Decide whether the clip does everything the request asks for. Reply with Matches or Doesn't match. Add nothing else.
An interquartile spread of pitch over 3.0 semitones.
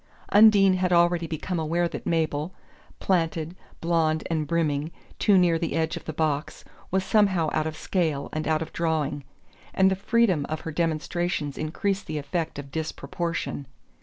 Doesn't match